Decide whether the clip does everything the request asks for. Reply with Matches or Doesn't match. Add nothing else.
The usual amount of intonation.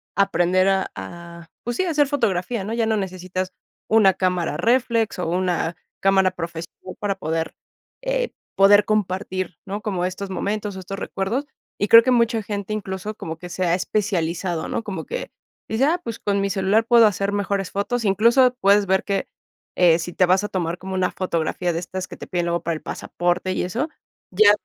Matches